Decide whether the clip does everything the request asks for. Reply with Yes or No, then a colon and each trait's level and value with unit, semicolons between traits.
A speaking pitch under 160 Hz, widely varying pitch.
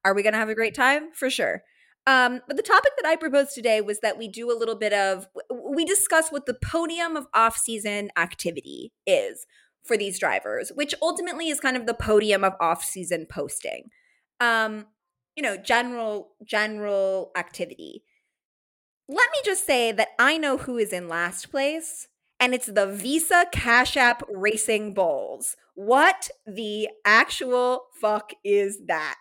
No: high, 235 Hz; wide, 5.7 semitones